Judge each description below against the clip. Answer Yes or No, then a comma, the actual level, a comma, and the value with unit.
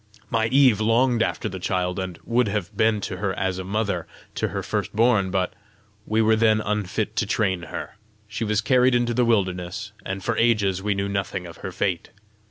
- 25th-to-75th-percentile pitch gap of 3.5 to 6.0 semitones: No, average, 3.1 semitones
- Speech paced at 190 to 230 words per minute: Yes, average, 200 wpm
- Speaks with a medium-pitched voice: No, low, 105 Hz